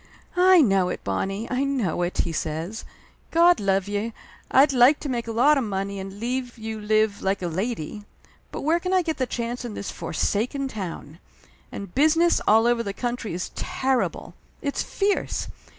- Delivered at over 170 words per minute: Yes, average, 180 wpm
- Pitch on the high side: Yes, high, 230 Hz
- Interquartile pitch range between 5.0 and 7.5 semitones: Yes, wide, 5.5 semitones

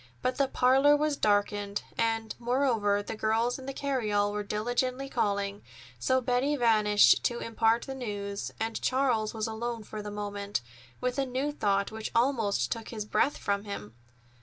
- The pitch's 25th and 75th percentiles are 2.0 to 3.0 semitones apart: No, average, 3.6 semitones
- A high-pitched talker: Yes, high, 225 Hz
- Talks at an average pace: Yes, average, 165 wpm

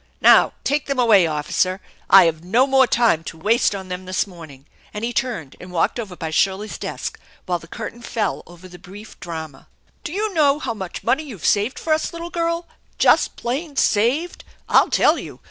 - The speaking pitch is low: No, high, 210 Hz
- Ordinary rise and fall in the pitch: No, wide, 7.2 semitones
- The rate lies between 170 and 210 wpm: Yes, average, 195 wpm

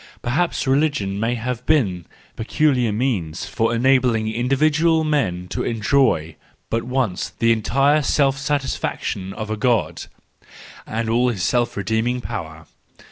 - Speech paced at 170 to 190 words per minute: No, slow, 135 wpm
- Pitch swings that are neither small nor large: Yes, average, 4.1 semitones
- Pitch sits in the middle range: No, low, 120 Hz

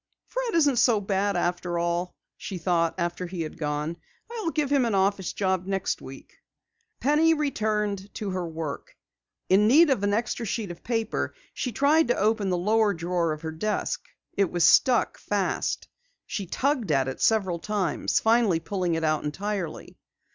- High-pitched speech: Yes, high, 195 Hz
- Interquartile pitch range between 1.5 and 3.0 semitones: No, average, 4.7 semitones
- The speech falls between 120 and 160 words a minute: No, average, 170 wpm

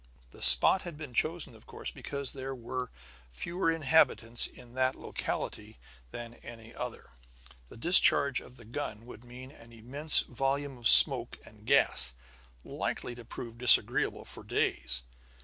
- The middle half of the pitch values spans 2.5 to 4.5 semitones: Yes, average, 3.4 semitones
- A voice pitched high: No, low, 125 Hz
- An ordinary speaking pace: Yes, average, 150 wpm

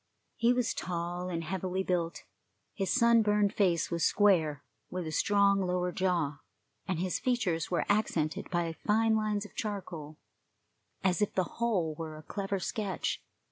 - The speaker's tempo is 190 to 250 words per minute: No, average, 150 wpm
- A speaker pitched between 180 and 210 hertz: Yes, medium, 185 Hz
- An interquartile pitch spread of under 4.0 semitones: Yes, average, 3.5 semitones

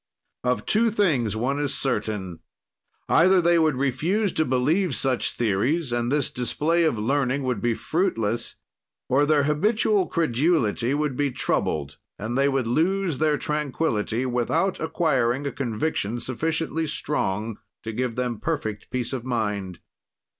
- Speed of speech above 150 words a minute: No, average, 140 wpm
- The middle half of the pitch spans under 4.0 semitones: No, average, 5.2 semitones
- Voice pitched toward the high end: No, low, 135 Hz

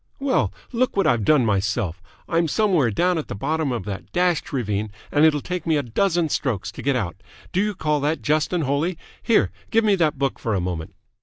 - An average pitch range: No, wide, 8.0 semitones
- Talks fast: Yes, fast, 220 wpm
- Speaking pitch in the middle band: Yes, medium, 150 Hz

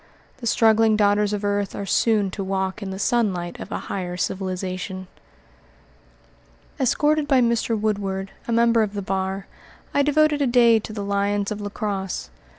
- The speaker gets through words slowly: No, average, 165 wpm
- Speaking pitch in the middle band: No, high, 205 Hz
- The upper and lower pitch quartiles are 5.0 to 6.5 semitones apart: No, average, 3.2 semitones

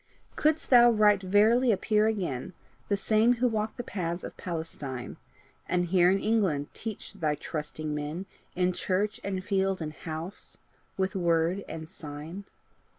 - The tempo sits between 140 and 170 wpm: Yes, average, 150 wpm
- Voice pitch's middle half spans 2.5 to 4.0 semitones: No, average, 4.7 semitones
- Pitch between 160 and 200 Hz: Yes, high, 190 Hz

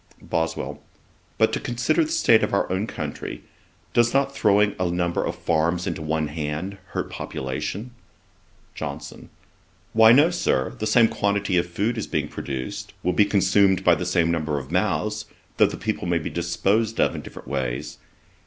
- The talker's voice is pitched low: Yes, very low, 90 Hz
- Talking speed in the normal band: Yes, average, 170 wpm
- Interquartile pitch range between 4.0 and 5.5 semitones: Yes, average, 4.9 semitones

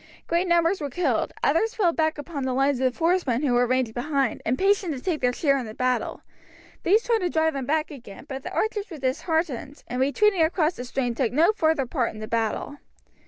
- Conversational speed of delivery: No, fast, 215 wpm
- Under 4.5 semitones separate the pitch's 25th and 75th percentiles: No, average, 5.1 semitones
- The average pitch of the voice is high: Yes, very high, 285 Hz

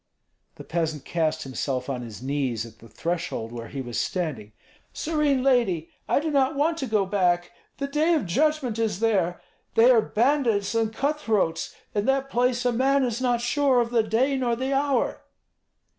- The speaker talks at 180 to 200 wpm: Yes, average, 185 wpm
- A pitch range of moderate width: No, wide, 8.2 semitones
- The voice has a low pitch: No, high, 225 Hz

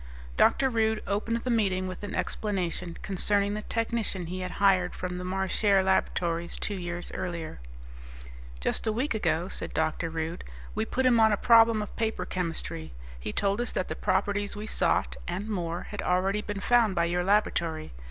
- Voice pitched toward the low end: No, high, 195 Hz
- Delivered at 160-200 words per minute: Yes, average, 180 wpm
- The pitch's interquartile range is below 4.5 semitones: Yes, average, 3.4 semitones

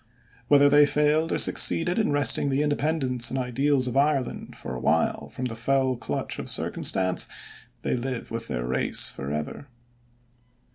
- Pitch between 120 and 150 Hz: Yes, low, 135 Hz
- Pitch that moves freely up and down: No, average, 3.6 semitones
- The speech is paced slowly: No, average, 155 wpm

